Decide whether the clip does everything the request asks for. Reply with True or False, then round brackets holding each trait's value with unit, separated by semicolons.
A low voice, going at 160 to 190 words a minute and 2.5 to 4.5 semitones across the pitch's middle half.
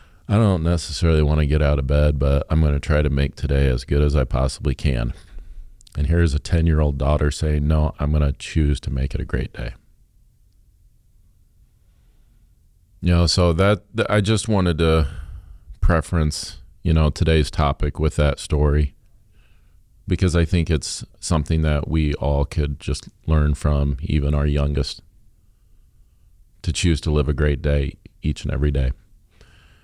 True (80 Hz; 170 wpm; 4.0 semitones)